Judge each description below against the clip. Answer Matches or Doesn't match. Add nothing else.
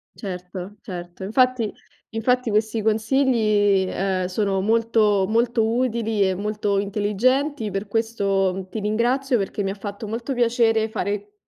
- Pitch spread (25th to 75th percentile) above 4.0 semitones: Doesn't match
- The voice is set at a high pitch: Matches